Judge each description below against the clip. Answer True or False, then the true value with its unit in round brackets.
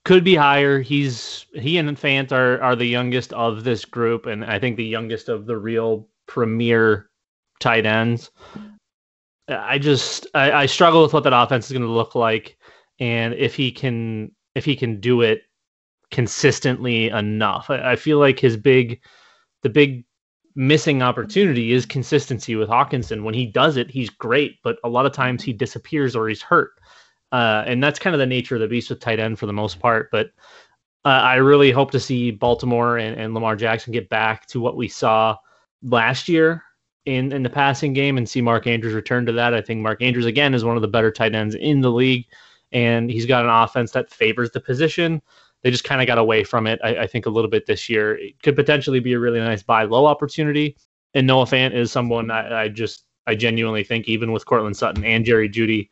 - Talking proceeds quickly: True (210 wpm)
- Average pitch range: True (3.2 semitones)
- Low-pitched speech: True (120 Hz)